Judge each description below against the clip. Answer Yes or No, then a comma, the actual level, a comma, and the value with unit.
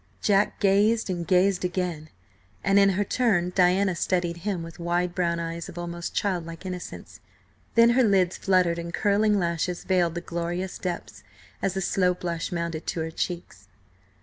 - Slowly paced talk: No, average, 165 wpm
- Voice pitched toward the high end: No, medium, 180 Hz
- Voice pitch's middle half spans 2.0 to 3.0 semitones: Yes, narrow, 2.4 semitones